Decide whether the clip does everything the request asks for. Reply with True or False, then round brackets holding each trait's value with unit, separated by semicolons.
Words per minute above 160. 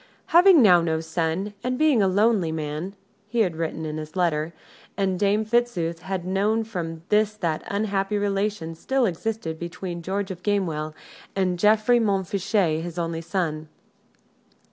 False (150 wpm)